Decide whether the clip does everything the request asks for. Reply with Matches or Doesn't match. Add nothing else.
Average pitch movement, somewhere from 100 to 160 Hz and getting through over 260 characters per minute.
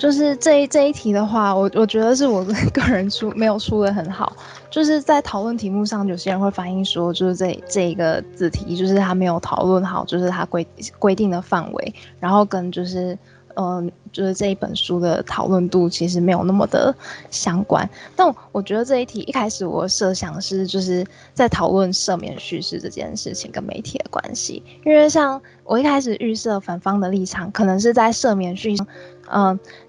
Doesn't match